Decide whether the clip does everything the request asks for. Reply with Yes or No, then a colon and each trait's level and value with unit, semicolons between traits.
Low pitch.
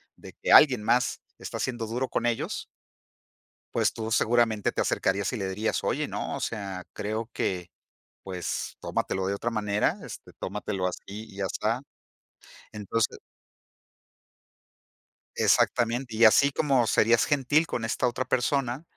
Yes: low, 115 Hz